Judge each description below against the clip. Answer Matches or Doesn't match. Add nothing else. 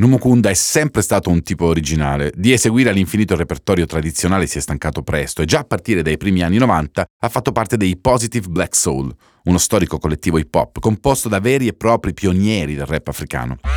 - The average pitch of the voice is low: Matches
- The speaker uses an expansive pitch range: Matches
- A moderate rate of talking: Doesn't match